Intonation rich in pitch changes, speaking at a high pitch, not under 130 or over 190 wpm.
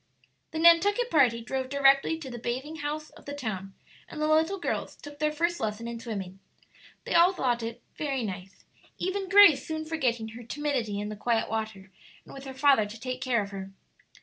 No: wide, 5.7 semitones; very high, 265 Hz; average, 200 wpm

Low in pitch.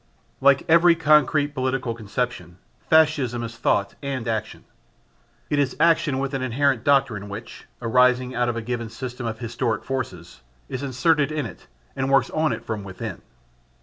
Yes: low, 125 Hz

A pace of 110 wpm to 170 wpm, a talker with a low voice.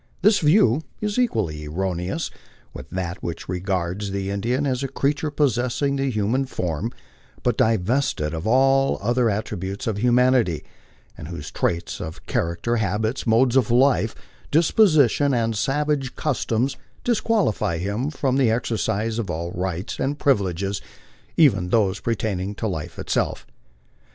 Yes: average, 140 wpm; low, 115 Hz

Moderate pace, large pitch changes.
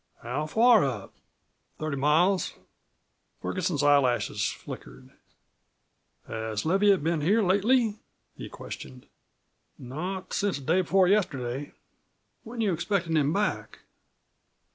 No: slow, 105 wpm; wide, 6.1 semitones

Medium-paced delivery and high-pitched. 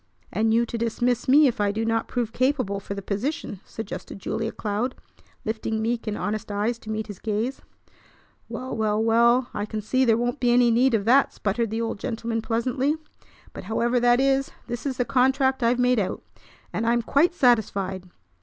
Yes: average, 190 wpm; high, 230 Hz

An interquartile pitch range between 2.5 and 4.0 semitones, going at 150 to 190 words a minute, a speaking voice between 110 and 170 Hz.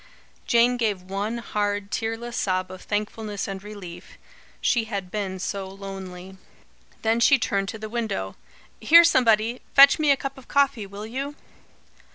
No: average, 3.4 semitones; average, 155 wpm; high, 215 Hz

